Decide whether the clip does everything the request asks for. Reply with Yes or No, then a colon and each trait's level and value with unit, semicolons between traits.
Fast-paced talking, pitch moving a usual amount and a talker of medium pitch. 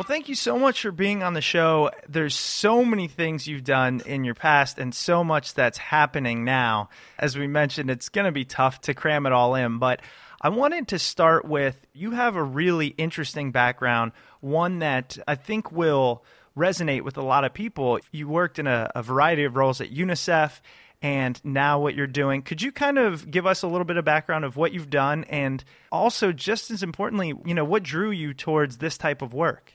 Yes: fast, 215 wpm; average, 4.5 semitones; medium, 150 Hz